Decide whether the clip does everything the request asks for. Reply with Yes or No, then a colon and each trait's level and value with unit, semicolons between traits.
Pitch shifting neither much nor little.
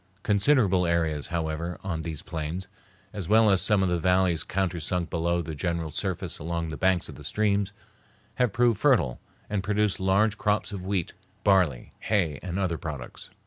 Yes: average, 3.4 semitones